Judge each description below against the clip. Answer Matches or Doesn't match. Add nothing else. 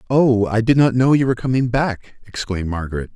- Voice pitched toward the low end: Matches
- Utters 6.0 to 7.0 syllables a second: Matches